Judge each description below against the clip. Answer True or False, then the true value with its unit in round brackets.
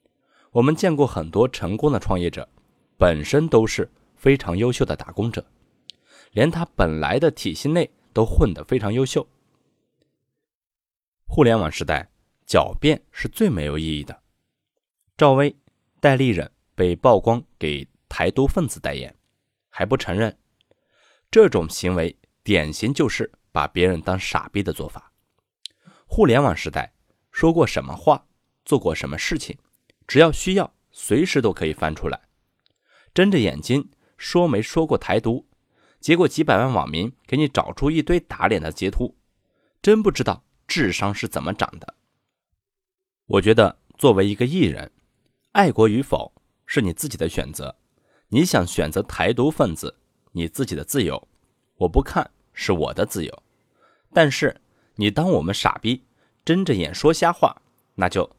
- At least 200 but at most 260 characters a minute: True (220 characters per minute)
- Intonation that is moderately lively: False (8.5 semitones)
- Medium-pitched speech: False (115 Hz)